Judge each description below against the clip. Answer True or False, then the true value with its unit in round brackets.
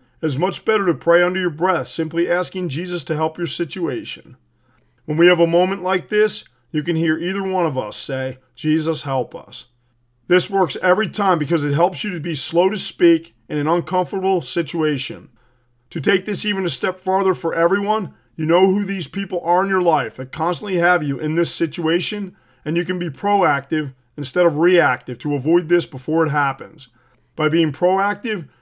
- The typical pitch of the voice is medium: True (170 Hz)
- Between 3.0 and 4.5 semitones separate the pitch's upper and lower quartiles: True (3.3 semitones)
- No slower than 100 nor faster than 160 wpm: False (195 wpm)